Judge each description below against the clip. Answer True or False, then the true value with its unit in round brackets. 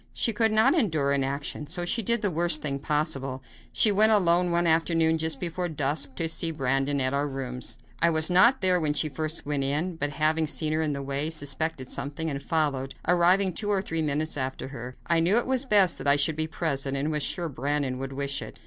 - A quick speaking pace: True (225 wpm)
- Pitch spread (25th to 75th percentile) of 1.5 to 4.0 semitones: True (3.7 semitones)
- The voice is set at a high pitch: False (155 Hz)